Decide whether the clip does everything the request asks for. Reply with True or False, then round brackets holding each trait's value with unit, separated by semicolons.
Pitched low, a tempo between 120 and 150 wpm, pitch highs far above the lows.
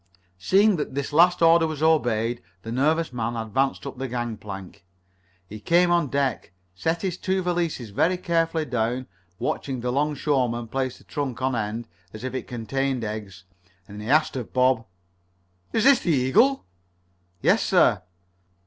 False (130 Hz; 165 wpm; 5.8 semitones)